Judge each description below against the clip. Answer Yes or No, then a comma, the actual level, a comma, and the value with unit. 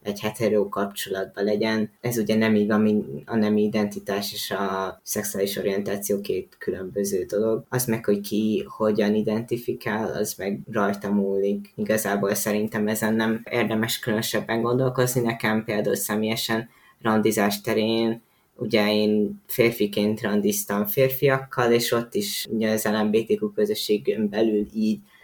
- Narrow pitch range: Yes, narrow, 1.6 semitones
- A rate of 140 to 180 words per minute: No, average, 130 wpm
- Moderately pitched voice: No, low, 110 Hz